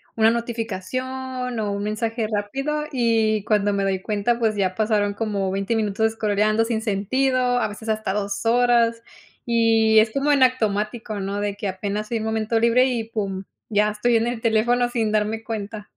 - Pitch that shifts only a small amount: Yes, narrow, 2.2 semitones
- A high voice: Yes, high, 220 Hz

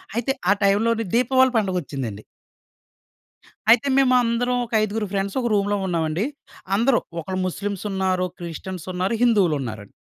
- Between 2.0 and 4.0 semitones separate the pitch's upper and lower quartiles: No, average, 4.4 semitones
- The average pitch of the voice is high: Yes, high, 200 Hz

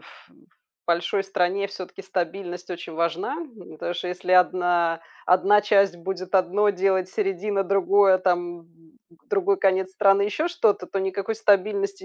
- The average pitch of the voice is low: No, high, 190 Hz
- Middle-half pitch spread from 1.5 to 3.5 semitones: Yes, narrow, 2.4 semitones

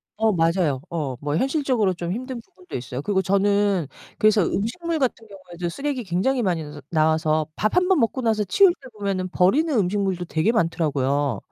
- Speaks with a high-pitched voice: Yes, high, 195 Hz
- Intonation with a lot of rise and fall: Yes, wide, 6.0 semitones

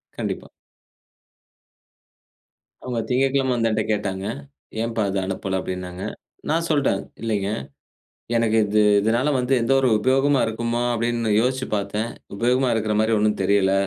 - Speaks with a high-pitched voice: No, low, 115 Hz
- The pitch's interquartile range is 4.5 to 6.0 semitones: No, average, 3.7 semitones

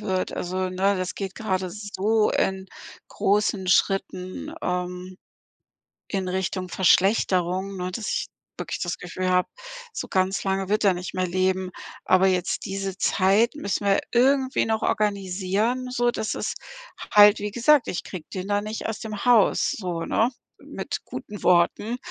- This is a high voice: Yes, high, 195 Hz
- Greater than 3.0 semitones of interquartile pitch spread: No, narrow, 2.4 semitones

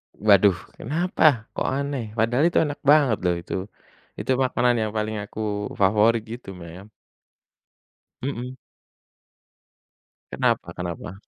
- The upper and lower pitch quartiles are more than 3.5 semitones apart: Yes, average, 4.3 semitones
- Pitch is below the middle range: Yes, low, 110 Hz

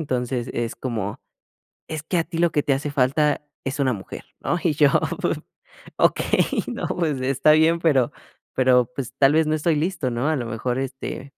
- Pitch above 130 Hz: Yes, medium, 140 Hz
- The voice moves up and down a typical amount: Yes, average, 3.6 semitones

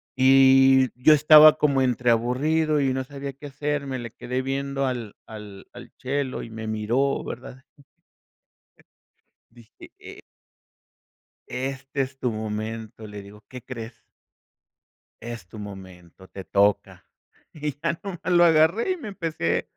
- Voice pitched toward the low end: Yes, low, 130 Hz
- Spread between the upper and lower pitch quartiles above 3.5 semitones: Yes, average, 4.2 semitones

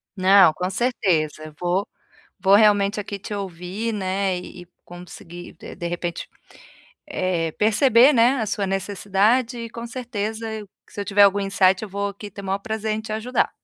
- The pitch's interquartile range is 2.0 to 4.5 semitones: Yes, average, 2.9 semitones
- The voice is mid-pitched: No, high, 200 Hz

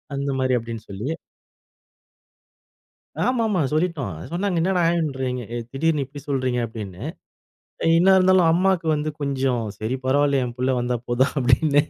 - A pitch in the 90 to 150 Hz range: Yes, medium, 140 Hz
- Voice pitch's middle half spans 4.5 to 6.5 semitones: Yes, average, 5.0 semitones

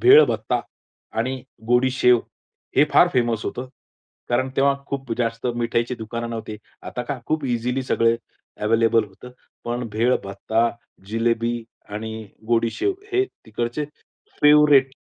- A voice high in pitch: No, low, 120 Hz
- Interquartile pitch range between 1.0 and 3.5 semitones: Yes, narrow, 2.4 semitones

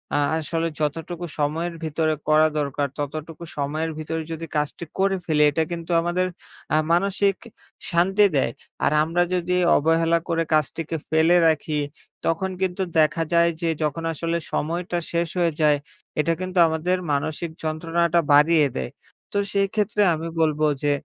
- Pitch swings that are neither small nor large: No, narrow, 2.0 semitones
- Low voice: No, medium, 165 Hz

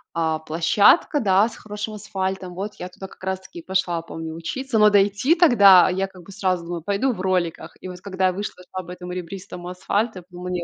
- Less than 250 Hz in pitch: Yes, medium, 185 Hz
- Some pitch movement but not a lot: No, narrow, 2.3 semitones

